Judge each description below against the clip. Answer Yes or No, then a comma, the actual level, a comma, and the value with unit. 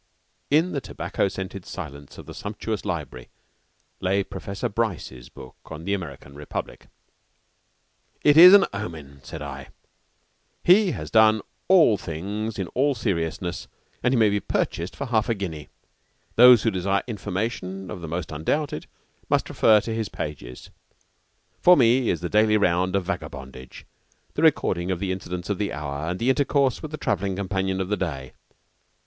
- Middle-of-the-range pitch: No, very low, 95 Hz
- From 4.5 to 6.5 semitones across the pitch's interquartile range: Yes, average, 5.2 semitones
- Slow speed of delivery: No, average, 160 wpm